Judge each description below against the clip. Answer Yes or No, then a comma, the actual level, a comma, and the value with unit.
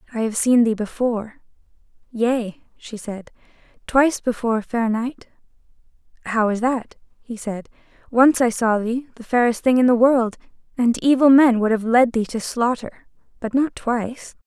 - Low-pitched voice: No, high, 235 Hz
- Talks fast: No, average, 160 wpm